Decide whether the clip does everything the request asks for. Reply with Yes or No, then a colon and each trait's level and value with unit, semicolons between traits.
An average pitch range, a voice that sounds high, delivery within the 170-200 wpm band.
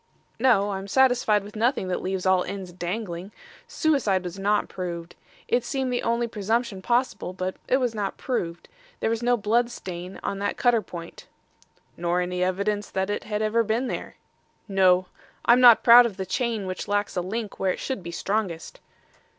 Yes: average, 4.1 semitones; high, 205 Hz; average, 185 wpm